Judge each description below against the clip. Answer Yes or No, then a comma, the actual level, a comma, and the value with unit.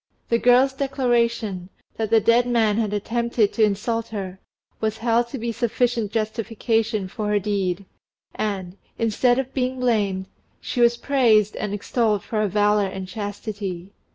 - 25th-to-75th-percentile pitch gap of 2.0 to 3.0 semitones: Yes, narrow, 2.6 semitones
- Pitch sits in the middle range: No, high, 220 Hz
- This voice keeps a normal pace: Yes, average, 155 wpm